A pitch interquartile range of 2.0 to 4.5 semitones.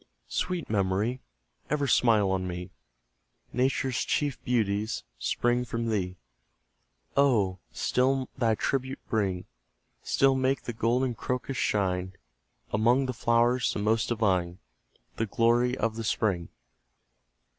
Yes: average, 4.2 semitones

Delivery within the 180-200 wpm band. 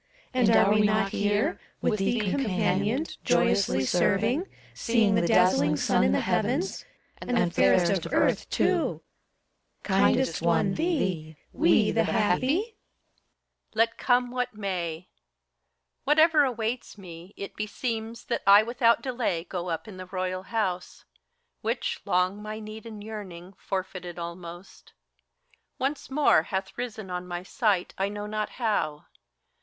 No: average, 150 wpm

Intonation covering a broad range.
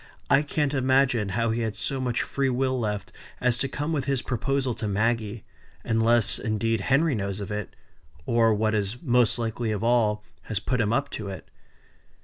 No: average, 3.5 semitones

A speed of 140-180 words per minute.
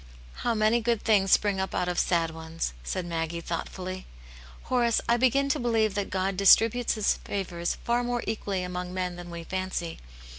No: average, 190 wpm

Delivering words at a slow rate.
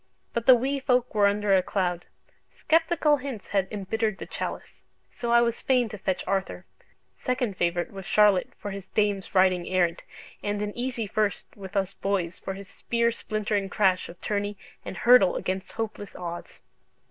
No: average, 170 wpm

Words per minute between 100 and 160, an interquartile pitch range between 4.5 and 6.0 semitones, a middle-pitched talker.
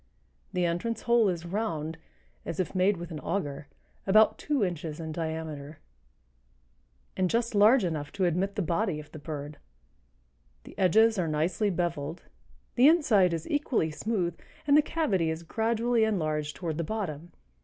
Yes: average, 155 wpm; wide, 5.5 semitones; medium, 175 Hz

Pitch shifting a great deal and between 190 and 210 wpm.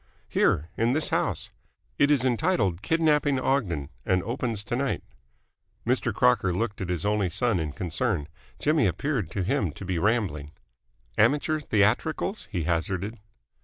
No: wide, 7.3 semitones; average, 145 wpm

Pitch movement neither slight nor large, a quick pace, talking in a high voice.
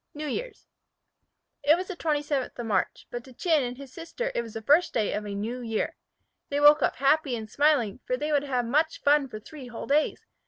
Yes: average, 4.1 semitones; fast, 225 wpm; very high, 280 Hz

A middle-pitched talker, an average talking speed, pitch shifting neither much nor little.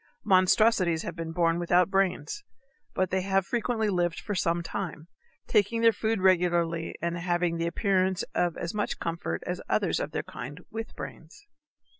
Yes: medium, 180 Hz; average, 165 wpm; average, 3.1 semitones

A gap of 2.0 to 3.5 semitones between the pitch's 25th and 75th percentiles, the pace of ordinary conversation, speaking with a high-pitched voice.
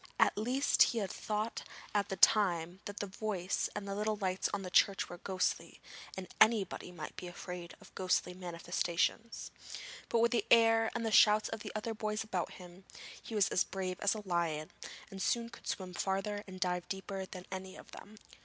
Yes: average, 2.9 semitones; average, 190 wpm; high, 195 Hz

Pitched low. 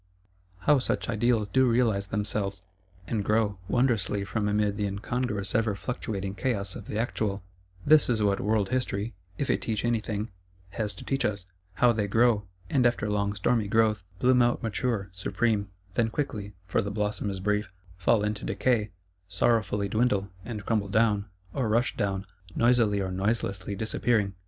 Yes: low, 105 Hz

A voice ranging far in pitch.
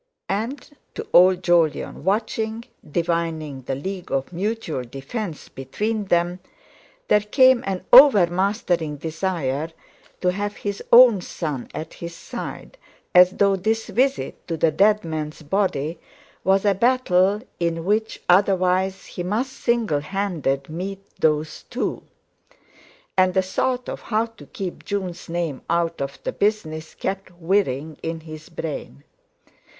No: average, 4.4 semitones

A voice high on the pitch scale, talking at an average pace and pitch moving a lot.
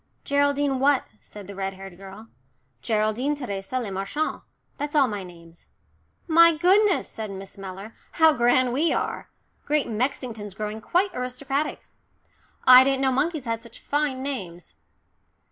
Yes: very high, 250 Hz; average, 145 wpm; wide, 6.0 semitones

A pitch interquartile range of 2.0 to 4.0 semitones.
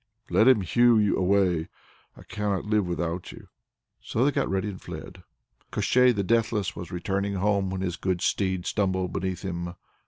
Yes: narrow, 2.6 semitones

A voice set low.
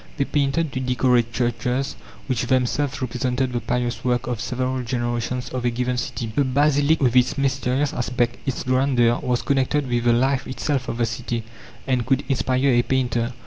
Yes: low, 125 Hz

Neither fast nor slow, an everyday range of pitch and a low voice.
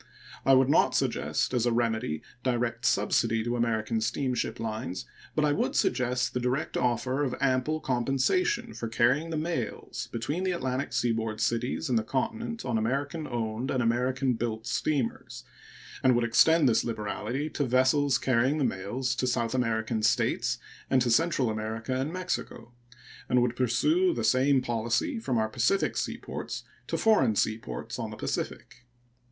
Yes: average, 160 wpm; average, 3.0 semitones; low, 125 Hz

